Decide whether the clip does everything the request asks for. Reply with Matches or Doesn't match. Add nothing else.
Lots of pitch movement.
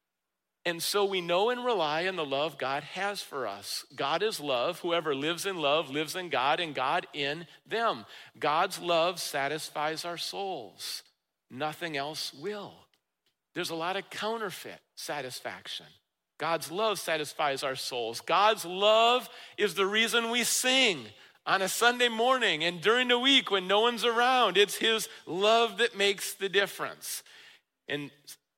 Matches